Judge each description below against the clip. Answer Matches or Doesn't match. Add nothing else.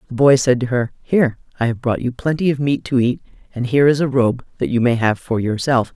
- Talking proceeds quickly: Matches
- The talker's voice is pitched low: Matches